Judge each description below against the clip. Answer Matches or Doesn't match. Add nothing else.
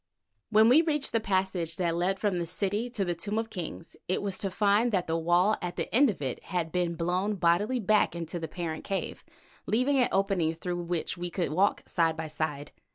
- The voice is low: Doesn't match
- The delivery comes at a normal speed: Doesn't match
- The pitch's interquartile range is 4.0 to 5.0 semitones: Doesn't match